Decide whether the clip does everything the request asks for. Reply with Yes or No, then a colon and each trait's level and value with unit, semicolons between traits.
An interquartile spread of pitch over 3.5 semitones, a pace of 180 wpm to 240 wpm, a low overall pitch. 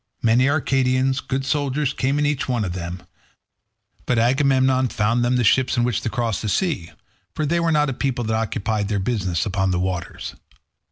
Yes: average, 4.2 semitones; average, 190 wpm; low, 125 Hz